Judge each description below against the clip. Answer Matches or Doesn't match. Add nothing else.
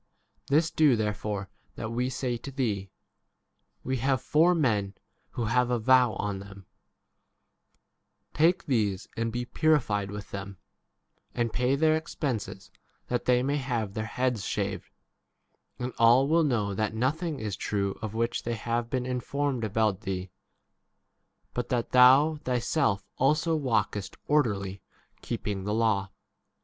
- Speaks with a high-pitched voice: Doesn't match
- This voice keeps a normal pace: Matches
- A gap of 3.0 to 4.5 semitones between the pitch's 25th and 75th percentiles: Matches